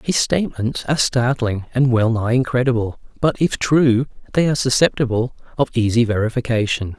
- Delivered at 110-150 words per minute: Yes, average, 145 wpm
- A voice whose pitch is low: Yes, low, 125 Hz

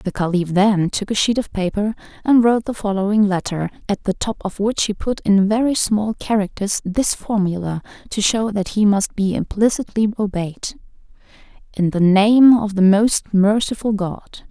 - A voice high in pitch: Yes, high, 205 Hz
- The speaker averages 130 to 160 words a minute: No, average, 170 wpm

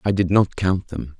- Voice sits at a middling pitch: No, very low, 90 Hz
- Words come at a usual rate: No, fast, 250 wpm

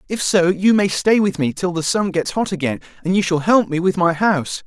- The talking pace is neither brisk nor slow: No, fast, 270 wpm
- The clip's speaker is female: No, male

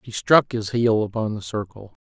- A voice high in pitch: No, low, 110 Hz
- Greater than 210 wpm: No, fast, 205 wpm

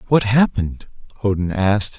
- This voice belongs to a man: Yes, male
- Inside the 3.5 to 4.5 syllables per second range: No, 5.5 syllables/s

